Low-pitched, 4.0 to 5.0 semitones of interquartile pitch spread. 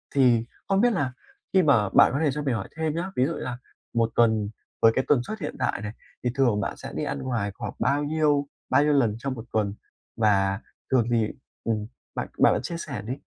Yes: low, 125 Hz; average, 4.7 semitones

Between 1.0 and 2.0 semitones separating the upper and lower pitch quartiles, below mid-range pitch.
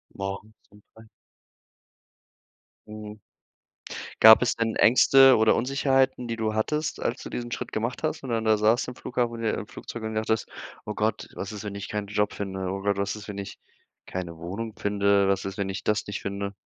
No: narrow, 2.4 semitones; low, 110 Hz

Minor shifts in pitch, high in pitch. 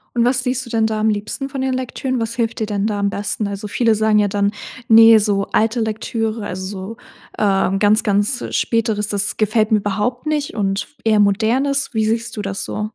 Yes: narrow, 2.3 semitones; high, 220 Hz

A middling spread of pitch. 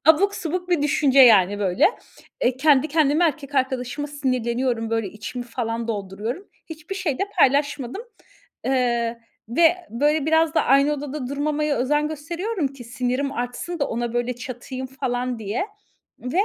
Yes: average, 3.9 semitones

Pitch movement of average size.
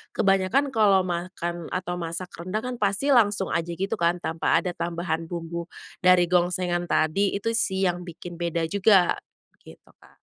No: narrow, 2.3 semitones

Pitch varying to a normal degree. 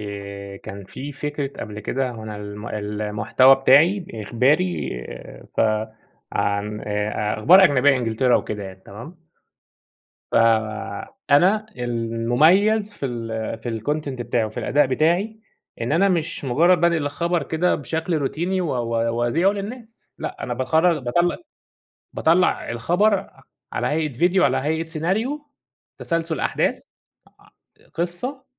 No: wide, 7.3 semitones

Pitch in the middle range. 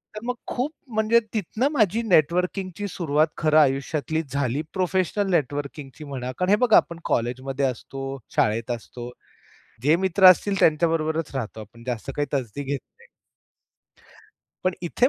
Yes: medium, 155 Hz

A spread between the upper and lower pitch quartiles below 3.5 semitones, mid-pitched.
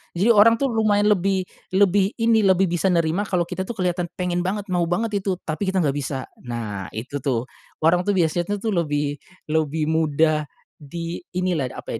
No: average, 4.4 semitones; medium, 175 Hz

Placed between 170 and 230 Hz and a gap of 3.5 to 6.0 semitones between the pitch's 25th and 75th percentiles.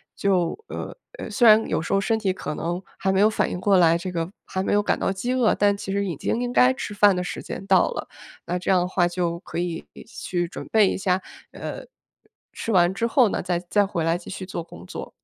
No: high, 190 Hz; average, 2.9 semitones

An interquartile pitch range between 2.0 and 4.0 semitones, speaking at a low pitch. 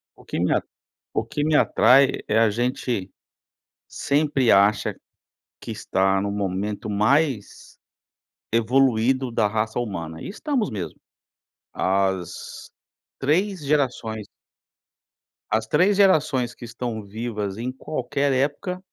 No: average, 5.3 semitones; low, 120 Hz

